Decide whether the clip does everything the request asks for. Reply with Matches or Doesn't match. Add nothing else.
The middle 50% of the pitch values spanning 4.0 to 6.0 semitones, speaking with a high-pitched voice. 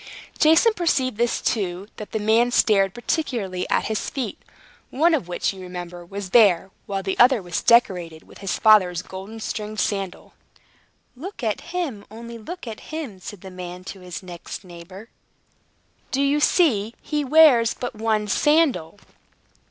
Matches